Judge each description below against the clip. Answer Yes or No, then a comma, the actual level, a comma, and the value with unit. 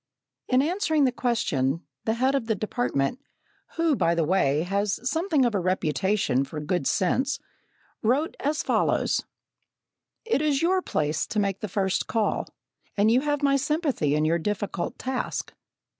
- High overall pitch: Yes, high, 220 Hz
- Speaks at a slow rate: No, average, 160 wpm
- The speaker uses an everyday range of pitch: No, wide, 8.0 semitones